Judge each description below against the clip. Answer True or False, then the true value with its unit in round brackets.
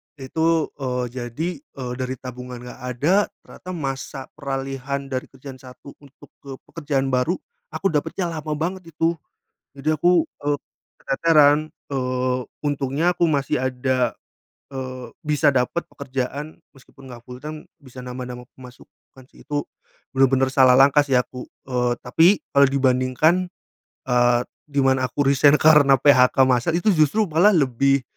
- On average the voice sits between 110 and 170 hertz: True (135 Hz)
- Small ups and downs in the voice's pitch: False (3.0 semitones)